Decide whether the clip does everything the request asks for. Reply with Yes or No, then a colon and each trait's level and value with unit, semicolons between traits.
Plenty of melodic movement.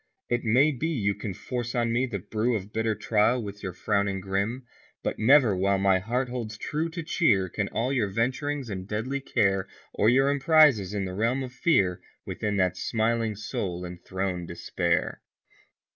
No: average, 4.5 semitones